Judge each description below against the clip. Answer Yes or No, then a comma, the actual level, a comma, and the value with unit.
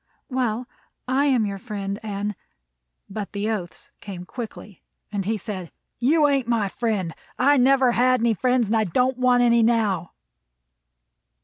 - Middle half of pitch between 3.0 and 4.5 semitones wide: Yes, average, 4.0 semitones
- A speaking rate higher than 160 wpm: No, average, 155 wpm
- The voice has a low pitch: No, high, 225 Hz